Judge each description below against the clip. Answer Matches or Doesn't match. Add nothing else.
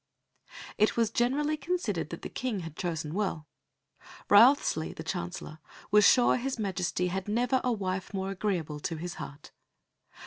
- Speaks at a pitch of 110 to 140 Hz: Doesn't match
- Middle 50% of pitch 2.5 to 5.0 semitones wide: Doesn't match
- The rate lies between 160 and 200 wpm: Doesn't match